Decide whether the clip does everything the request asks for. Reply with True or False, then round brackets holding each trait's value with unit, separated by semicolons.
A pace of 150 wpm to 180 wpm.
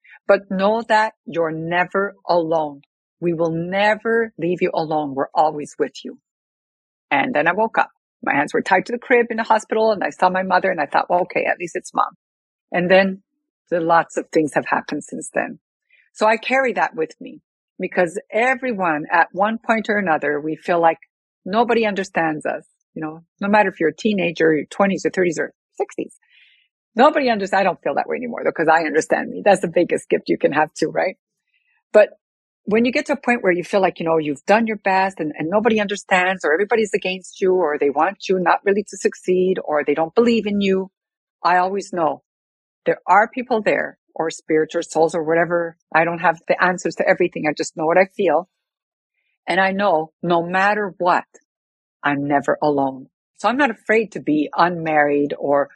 False (205 wpm)